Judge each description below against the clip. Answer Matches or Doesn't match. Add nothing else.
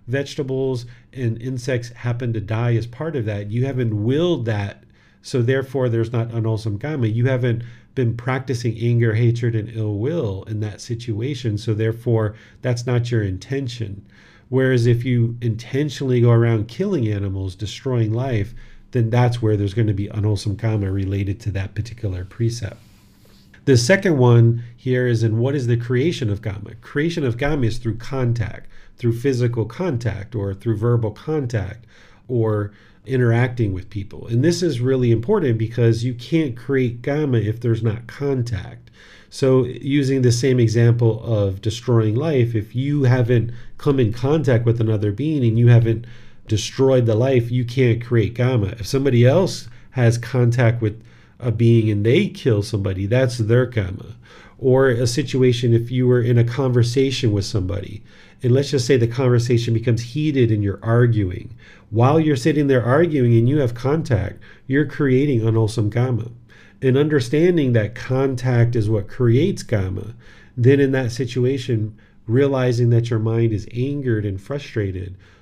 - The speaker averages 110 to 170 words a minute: Matches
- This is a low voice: Matches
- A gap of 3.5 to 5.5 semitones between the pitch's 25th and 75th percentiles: Doesn't match